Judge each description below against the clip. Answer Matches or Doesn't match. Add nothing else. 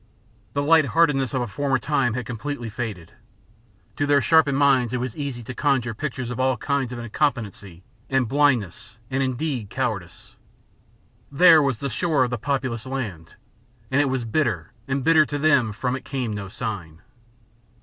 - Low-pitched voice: Matches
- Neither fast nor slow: Matches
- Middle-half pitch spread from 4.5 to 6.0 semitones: Doesn't match